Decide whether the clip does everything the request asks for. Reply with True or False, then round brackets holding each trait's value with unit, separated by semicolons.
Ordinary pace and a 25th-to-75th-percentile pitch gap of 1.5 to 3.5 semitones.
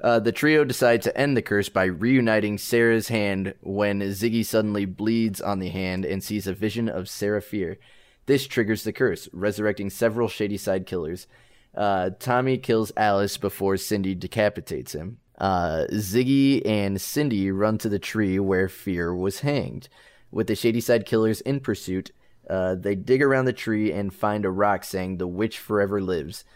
True (170 wpm; 3.1 semitones)